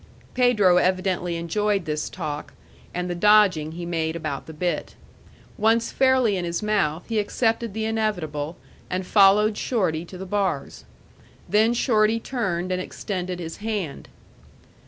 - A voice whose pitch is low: No, medium, 185 Hz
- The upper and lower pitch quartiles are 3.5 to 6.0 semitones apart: Yes, average, 4.0 semitones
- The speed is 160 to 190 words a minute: No, average, 140 wpm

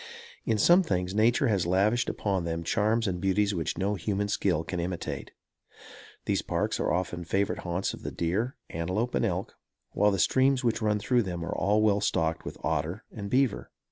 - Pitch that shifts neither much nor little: Yes, average, 3.6 semitones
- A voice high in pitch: No, low, 100 Hz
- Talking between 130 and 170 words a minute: No, average, 180 wpm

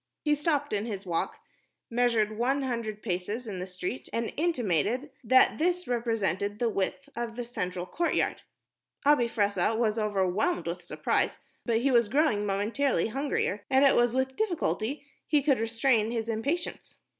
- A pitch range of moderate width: Yes, average, 4.6 semitones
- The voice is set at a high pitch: Yes, high, 230 Hz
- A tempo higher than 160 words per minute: No, average, 155 wpm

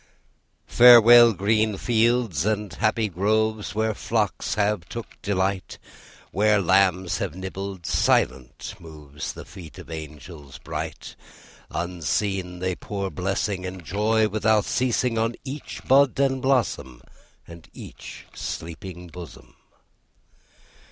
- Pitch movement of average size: Yes, average, 3.9 semitones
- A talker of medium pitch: No, low, 100 Hz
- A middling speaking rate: No, slow, 110 wpm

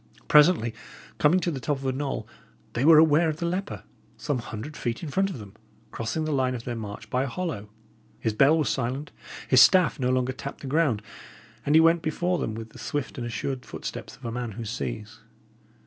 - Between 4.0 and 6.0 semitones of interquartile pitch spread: Yes, average, 5.1 semitones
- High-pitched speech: No, low, 135 Hz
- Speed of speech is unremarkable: No, fast, 215 wpm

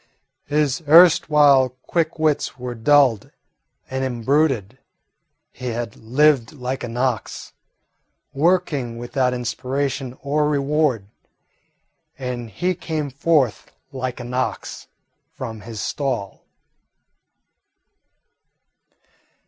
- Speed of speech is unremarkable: No, slow, 90 wpm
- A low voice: Yes, low, 130 Hz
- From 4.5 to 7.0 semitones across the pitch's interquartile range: No, average, 3.5 semitones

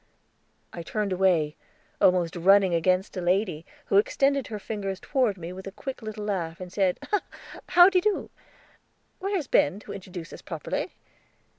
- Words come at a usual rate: Yes, average, 155 wpm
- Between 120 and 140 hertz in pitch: No, high, 195 Hz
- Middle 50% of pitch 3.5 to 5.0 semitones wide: Yes, average, 4.1 semitones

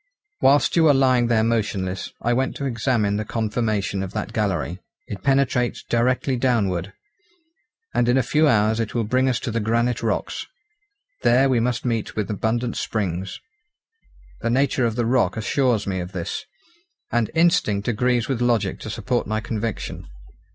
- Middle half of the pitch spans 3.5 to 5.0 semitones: No, average, 3.1 semitones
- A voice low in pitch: Yes, low, 115 Hz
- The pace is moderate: Yes, average, 165 wpm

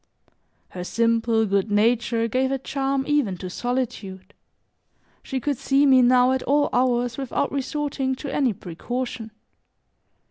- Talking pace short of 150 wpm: Yes, slow, 135 wpm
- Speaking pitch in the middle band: No, very high, 250 Hz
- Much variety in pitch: No, average, 3.1 semitones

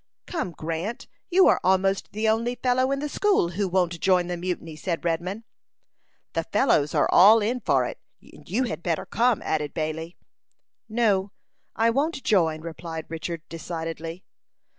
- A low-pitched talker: No, medium, 185 Hz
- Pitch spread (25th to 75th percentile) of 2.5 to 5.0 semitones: No, wide, 5.6 semitones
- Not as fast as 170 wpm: Yes, average, 160 wpm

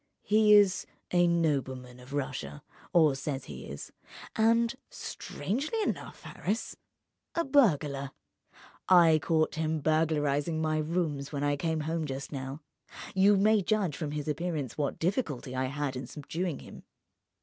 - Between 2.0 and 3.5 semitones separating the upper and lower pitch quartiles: No, average, 4.6 semitones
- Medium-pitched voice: Yes, medium, 155 Hz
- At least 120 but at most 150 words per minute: Yes, slow, 135 wpm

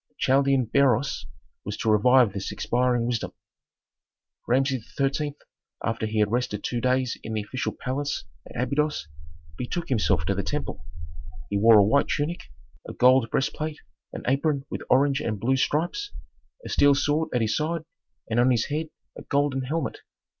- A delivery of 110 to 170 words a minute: Yes, average, 165 wpm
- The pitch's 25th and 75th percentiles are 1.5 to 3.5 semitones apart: No, average, 3.9 semitones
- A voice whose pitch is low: Yes, low, 130 Hz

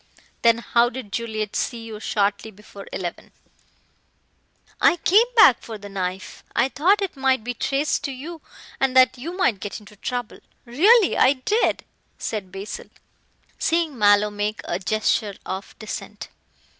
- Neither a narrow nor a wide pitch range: Yes, average, 4.8 semitones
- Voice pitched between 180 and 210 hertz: No, high, 230 Hz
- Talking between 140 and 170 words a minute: Yes, average, 150 wpm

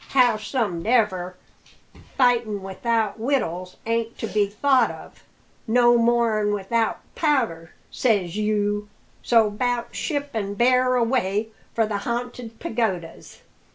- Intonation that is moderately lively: Yes, average, 3.0 semitones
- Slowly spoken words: Yes, slow, 110 wpm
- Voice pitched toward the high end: Yes, high, 225 Hz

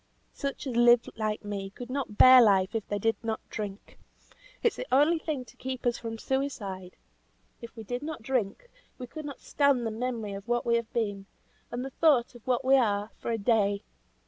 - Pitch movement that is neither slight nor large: Yes, average, 3.6 semitones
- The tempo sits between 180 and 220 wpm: Yes, fast, 205 wpm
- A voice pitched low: No, high, 235 Hz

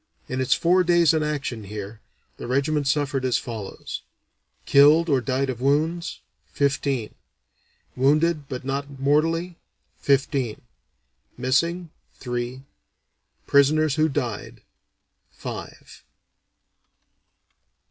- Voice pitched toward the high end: No, medium, 140 Hz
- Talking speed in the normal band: No, slow, 95 wpm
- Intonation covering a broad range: No, average, 3.2 semitones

